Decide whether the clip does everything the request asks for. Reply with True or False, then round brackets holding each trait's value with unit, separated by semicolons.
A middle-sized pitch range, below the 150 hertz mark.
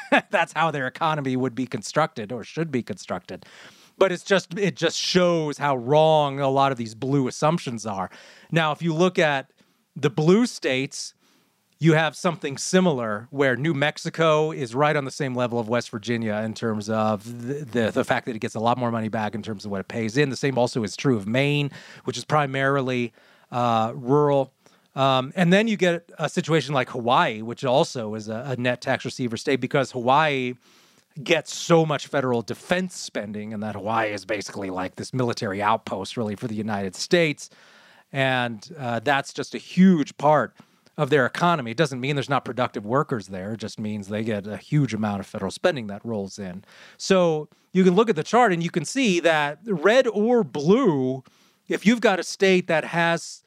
False (5.8 semitones; 135 Hz)